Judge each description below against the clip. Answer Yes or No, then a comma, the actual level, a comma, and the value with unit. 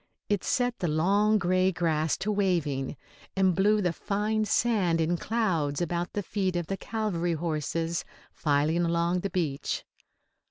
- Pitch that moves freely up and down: No, average, 3.6 semitones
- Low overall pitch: No, medium, 175 Hz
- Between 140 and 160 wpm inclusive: Yes, average, 150 wpm